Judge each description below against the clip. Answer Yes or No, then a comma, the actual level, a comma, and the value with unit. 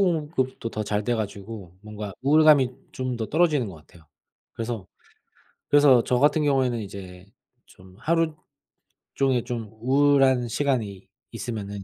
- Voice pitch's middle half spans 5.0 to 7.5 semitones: Yes, wide, 5.4 semitones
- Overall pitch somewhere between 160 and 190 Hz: No, low, 120 Hz